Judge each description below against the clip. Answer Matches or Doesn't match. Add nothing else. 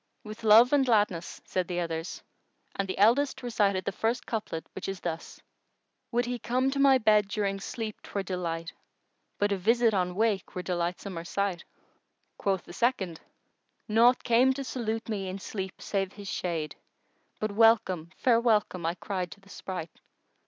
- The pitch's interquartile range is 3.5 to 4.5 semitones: Matches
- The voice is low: Doesn't match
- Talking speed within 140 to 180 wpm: Matches